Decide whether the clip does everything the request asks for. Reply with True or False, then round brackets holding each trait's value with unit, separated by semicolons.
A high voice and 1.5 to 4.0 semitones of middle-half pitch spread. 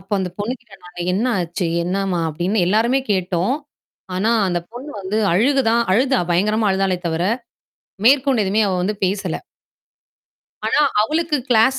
False (200 Hz; 4.8 semitones)